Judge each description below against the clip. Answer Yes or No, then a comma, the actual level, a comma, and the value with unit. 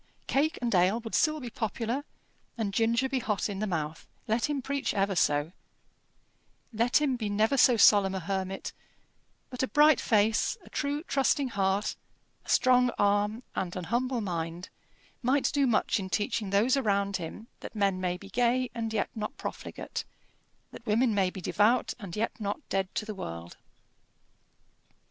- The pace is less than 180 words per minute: Yes, average, 170 wpm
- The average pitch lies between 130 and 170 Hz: No, high, 215 Hz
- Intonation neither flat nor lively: Yes, average, 4.3 semitones